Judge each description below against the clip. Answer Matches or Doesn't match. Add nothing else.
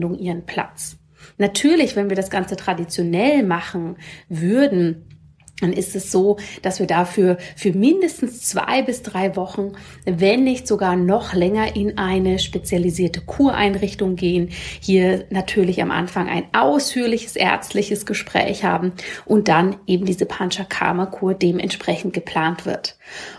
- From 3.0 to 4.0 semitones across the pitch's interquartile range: Doesn't match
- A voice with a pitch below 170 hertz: Doesn't match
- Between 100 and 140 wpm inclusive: Matches